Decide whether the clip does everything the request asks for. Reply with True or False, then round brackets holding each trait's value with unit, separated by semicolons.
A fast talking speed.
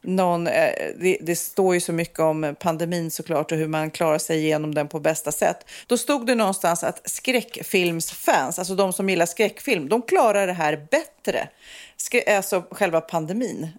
False (170 wpm)